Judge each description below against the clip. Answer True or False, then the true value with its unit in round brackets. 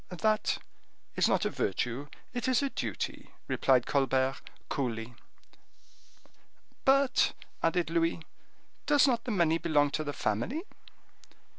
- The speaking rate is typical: False (120 wpm)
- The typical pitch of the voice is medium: True (165 Hz)